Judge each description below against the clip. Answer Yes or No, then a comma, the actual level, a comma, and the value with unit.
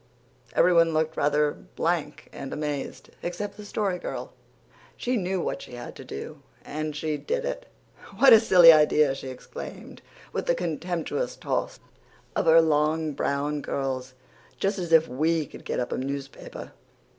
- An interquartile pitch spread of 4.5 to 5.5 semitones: No, average, 3.5 semitones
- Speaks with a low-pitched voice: No, medium, 160 Hz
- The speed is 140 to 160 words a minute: Yes, average, 155 wpm